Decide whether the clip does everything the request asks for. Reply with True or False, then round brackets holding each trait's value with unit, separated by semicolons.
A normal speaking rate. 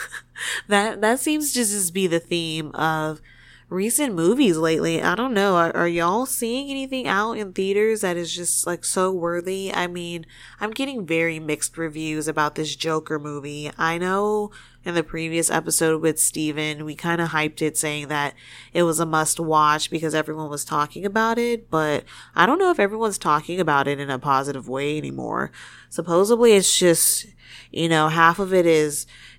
True (180 wpm)